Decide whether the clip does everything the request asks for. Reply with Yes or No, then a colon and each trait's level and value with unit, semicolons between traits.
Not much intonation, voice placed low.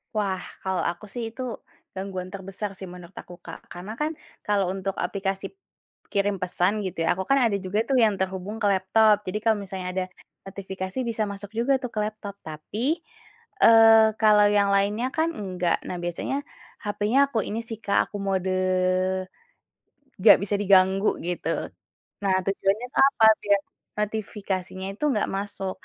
No: narrow, 2.2 semitones; high, 200 Hz